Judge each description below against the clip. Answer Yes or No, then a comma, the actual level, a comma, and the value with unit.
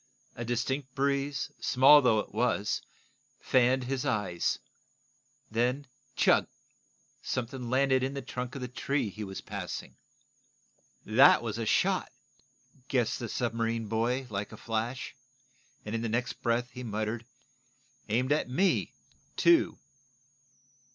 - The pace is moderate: No, slow, 130 wpm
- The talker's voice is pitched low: Yes, low, 125 Hz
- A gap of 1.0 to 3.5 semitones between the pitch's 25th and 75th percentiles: Yes, narrow, 2.6 semitones